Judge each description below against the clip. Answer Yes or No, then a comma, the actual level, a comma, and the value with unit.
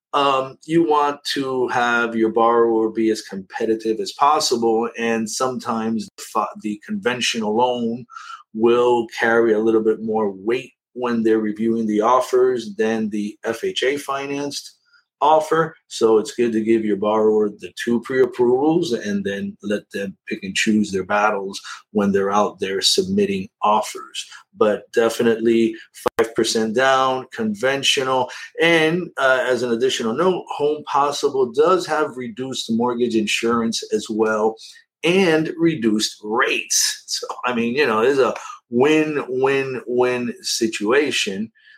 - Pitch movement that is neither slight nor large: No, wide, 6.5 semitones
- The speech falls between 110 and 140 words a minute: Yes, slow, 135 wpm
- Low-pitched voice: Yes, low, 125 Hz